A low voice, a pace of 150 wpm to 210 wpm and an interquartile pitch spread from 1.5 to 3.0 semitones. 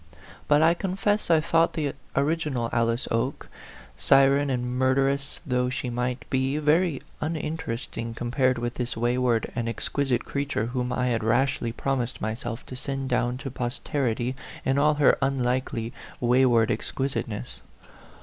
No: low, 130 Hz; average, 140 wpm; average, 2.7 semitones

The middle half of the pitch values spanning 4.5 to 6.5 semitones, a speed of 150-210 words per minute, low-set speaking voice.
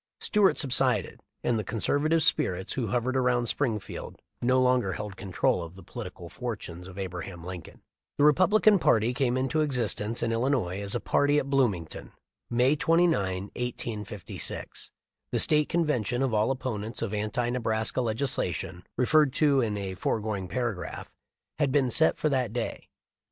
Yes: average, 4.9 semitones; average, 155 wpm; low, 120 Hz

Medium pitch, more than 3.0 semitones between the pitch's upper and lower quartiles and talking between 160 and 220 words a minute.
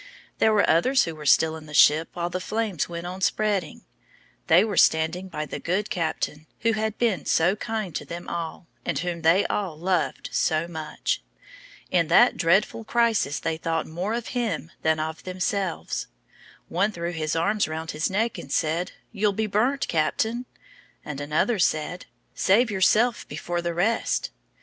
Yes: medium, 175 Hz; average, 4.8 semitones; average, 170 wpm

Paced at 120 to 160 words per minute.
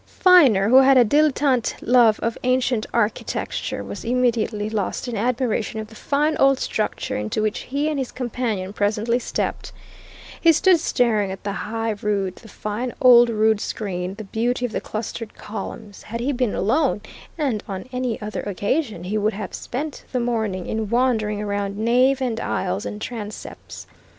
No: average, 170 wpm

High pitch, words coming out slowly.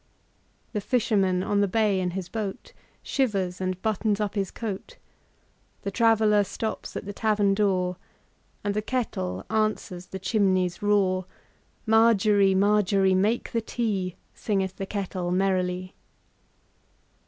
Yes: high, 200 Hz; slow, 110 wpm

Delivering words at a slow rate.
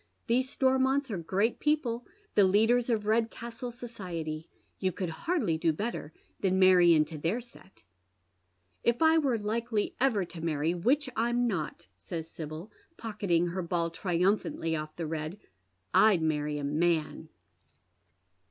No: average, 145 wpm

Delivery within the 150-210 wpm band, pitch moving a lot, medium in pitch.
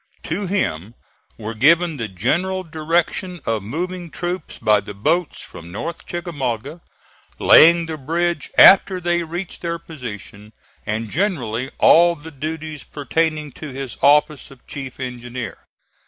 No: slow, 135 wpm; wide, 5.9 semitones; medium, 155 Hz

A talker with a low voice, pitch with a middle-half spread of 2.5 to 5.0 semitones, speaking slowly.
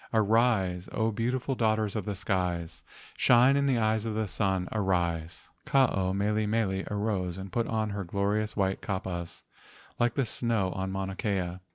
No: low, 105 Hz; average, 3.0 semitones; average, 170 wpm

